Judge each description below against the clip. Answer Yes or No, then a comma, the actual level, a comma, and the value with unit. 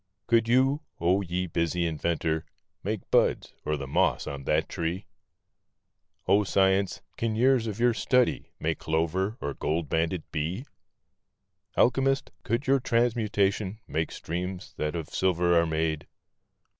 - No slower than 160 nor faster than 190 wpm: No, slow, 135 wpm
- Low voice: Yes, very low, 95 Hz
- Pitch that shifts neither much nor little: No, wide, 5.8 semitones